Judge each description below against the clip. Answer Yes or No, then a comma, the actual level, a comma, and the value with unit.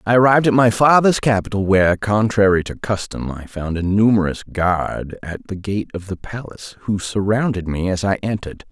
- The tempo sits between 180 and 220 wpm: Yes, average, 185 wpm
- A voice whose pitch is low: Yes, low, 100 Hz